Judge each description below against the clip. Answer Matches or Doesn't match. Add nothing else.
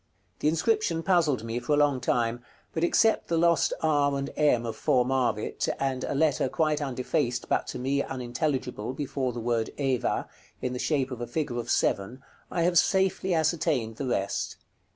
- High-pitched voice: Doesn't match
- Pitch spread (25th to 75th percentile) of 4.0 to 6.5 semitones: Matches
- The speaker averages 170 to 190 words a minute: Matches